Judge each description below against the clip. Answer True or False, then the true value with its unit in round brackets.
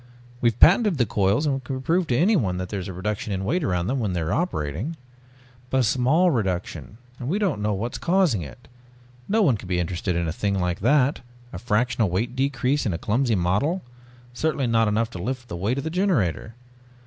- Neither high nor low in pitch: False (115 Hz)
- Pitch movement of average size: False (6.8 semitones)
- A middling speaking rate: False (220 wpm)